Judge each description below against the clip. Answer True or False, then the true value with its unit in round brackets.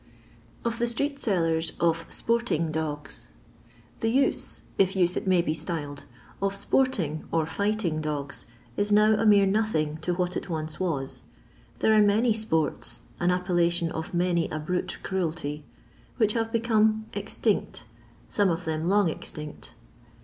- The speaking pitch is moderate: True (180 Hz)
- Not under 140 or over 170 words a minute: True (155 wpm)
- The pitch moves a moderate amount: True (5.0 semitones)